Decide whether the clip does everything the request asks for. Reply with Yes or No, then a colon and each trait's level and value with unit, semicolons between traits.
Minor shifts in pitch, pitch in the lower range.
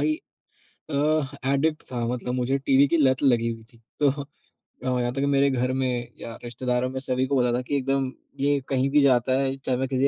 Yes: narrow, 1.9 semitones; low, 130 Hz